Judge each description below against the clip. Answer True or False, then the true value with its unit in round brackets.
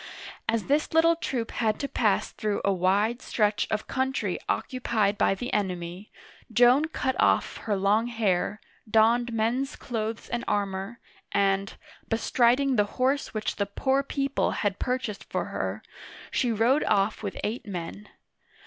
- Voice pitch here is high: True (225 Hz)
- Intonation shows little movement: False (3.8 semitones)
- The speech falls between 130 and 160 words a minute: True (150 wpm)